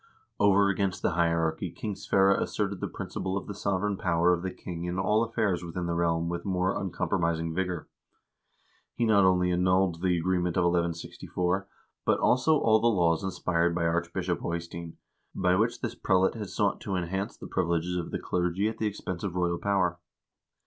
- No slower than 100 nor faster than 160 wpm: No, average, 180 wpm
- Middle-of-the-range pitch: No, very low, 90 Hz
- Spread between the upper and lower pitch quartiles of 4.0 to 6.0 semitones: No, narrow, 2.4 semitones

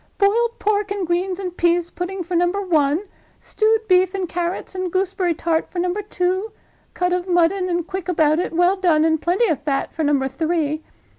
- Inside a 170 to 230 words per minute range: Yes, average, 195 wpm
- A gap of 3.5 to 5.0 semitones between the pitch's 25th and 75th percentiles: No, narrow, 2.5 semitones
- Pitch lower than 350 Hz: No, very high, 355 Hz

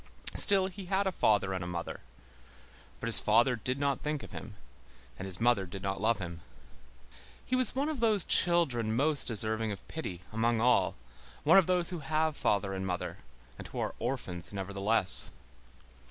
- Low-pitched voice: Yes, low, 115 Hz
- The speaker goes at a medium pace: Yes, average, 180 wpm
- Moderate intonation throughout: No, wide, 8.5 semitones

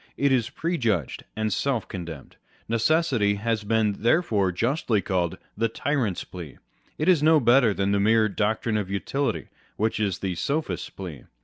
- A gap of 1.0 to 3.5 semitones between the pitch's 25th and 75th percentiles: No, average, 5.2 semitones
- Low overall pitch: Yes, low, 110 Hz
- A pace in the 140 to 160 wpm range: No, average, 170 wpm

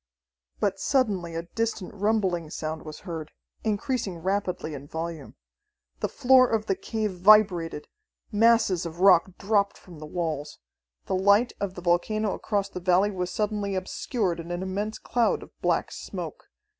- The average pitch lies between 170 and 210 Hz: Yes, high, 190 Hz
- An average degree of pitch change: Yes, average, 3.8 semitones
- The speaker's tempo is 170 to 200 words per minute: No, average, 155 wpm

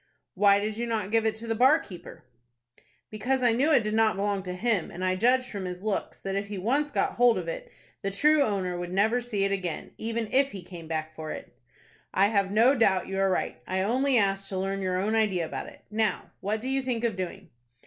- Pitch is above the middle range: Yes, high, 210 Hz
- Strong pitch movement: No, average, 3.8 semitones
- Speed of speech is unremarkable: No, fast, 240 wpm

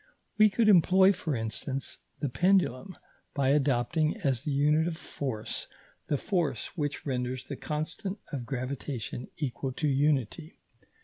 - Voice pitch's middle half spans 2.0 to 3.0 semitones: No, average, 4.0 semitones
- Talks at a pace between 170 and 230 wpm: No, slow, 135 wpm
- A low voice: No, medium, 145 Hz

